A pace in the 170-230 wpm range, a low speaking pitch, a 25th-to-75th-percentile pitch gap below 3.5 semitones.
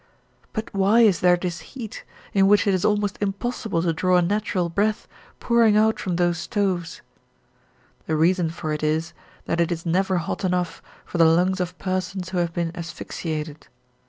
No: average, 180 wpm; medium, 180 Hz; average, 3.1 semitones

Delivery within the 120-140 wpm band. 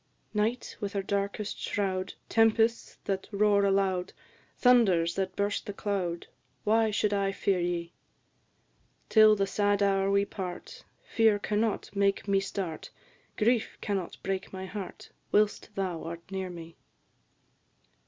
Yes: slow, 135 wpm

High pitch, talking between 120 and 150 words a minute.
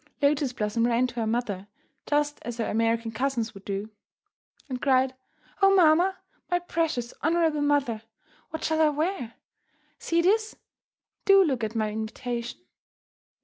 Yes: very high, 260 Hz; average, 145 wpm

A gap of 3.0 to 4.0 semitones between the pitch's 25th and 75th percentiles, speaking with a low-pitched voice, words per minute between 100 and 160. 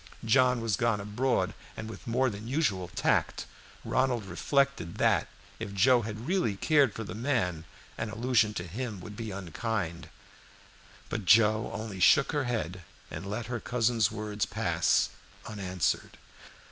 Yes: average, 3.7 semitones; low, 110 Hz; average, 145 wpm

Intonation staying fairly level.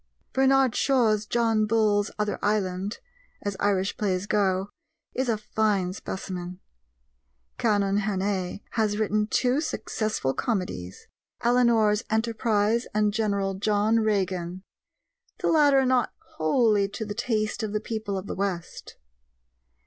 Yes: narrow, 2.3 semitones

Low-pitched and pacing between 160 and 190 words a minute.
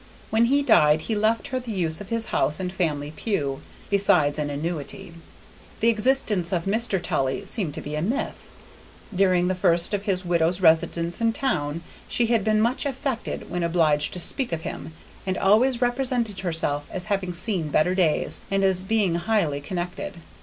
No: medium, 185 Hz; average, 180 wpm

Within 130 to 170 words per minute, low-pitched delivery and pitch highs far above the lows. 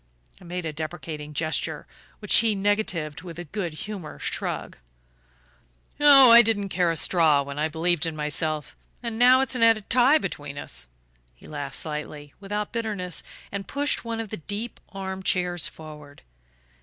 No: average, 165 wpm; medium, 180 Hz; wide, 5.8 semitones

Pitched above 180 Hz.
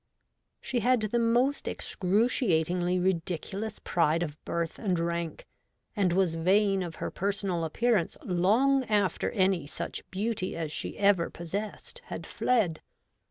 Yes: high, 190 Hz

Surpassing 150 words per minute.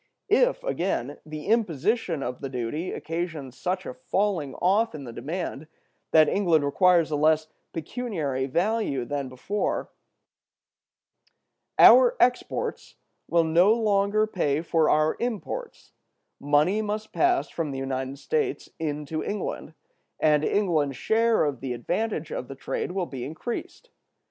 No: slow, 135 wpm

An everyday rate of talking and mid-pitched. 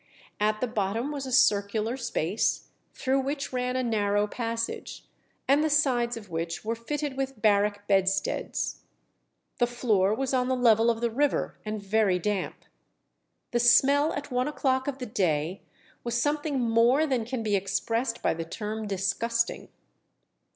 No: average, 160 wpm; high, 230 Hz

